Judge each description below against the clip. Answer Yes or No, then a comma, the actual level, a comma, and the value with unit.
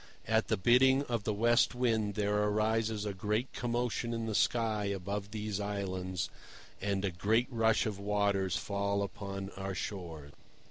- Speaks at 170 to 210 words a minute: No, average, 155 wpm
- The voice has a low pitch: Yes, low, 105 Hz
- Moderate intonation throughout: No, narrow, 2.3 semitones